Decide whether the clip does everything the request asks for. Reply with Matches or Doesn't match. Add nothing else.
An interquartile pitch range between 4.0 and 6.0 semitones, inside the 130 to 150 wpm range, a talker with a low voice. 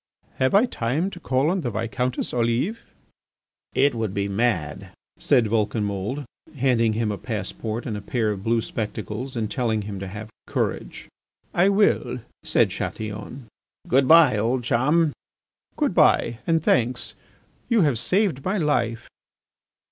Matches